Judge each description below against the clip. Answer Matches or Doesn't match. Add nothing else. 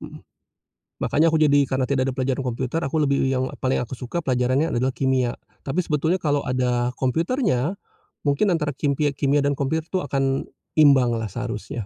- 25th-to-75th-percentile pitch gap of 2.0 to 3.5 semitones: Matches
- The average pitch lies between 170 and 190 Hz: Doesn't match